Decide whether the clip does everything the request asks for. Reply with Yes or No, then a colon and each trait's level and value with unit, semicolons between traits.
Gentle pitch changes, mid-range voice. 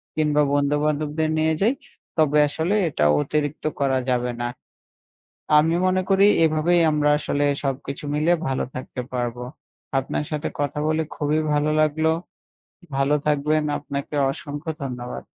Yes: narrow, 2.0 semitones; medium, 150 Hz